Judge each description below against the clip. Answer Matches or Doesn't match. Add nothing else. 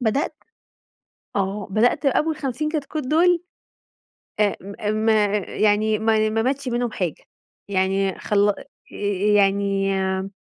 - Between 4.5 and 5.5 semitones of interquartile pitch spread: Matches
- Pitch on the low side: Doesn't match